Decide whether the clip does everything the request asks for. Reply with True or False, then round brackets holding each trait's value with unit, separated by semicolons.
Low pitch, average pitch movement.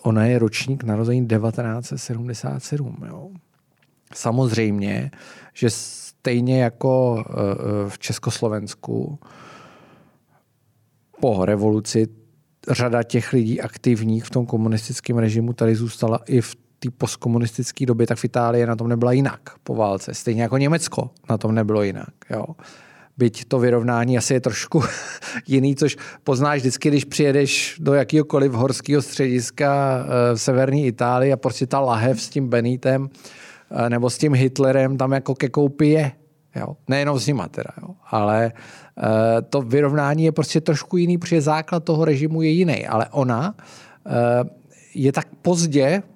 True (130 Hz; 3.5 semitones)